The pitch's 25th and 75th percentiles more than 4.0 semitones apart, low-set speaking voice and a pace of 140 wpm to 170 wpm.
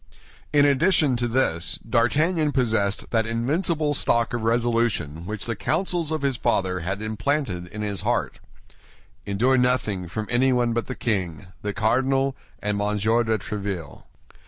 Yes: average, 4.6 semitones; low, 115 Hz; average, 145 wpm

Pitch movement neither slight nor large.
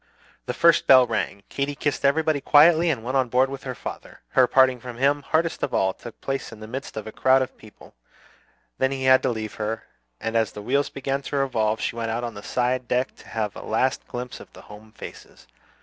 Yes: average, 3.4 semitones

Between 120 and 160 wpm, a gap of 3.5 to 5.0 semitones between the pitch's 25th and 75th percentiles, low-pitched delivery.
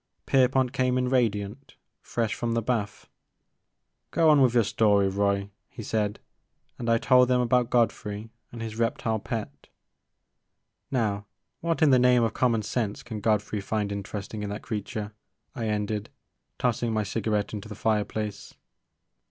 No: average, 155 wpm; average, 3.0 semitones; low, 110 Hz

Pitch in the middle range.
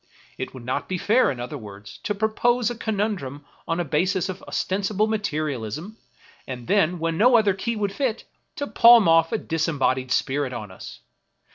Yes: medium, 175 Hz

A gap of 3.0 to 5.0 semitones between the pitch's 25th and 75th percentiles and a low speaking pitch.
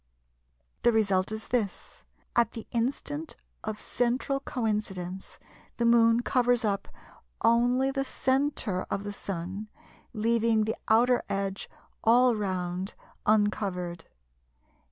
No: average, 3.6 semitones; high, 220 Hz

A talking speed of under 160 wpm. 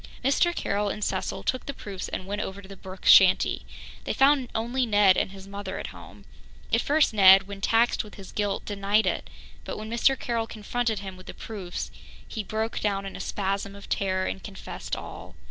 No: fast, 205 wpm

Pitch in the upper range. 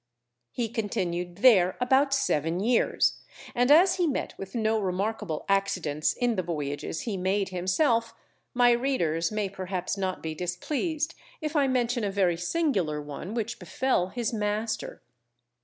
Yes: high, 205 Hz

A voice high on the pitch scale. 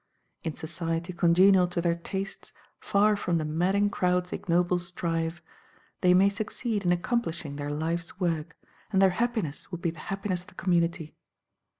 No: medium, 175 Hz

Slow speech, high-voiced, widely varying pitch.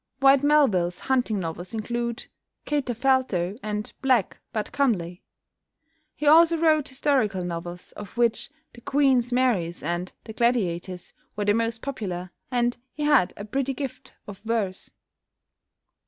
Yes: slow, 130 wpm; high, 230 Hz; wide, 6.1 semitones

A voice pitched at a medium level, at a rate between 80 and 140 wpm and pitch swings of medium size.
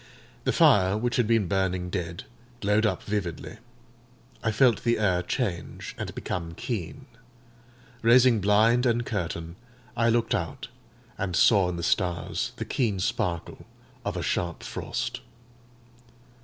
No: low, 100 Hz; slow, 135 wpm; average, 4.6 semitones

